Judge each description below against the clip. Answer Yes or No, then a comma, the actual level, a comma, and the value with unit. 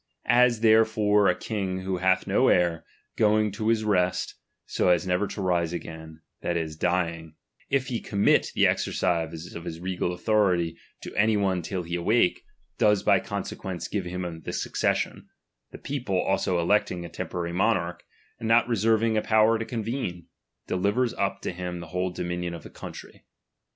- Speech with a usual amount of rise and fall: Yes, average, 3.7 semitones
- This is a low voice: Yes, very low, 95 Hz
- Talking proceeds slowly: No, average, 170 wpm